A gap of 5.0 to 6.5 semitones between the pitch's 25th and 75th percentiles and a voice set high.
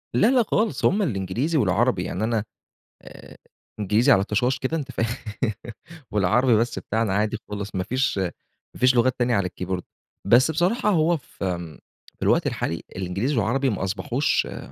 No: wide, 5.6 semitones; low, 115 Hz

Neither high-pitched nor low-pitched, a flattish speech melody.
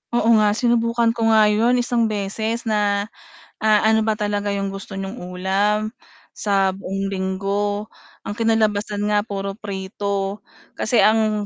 No: high, 210 Hz; narrow, 1.9 semitones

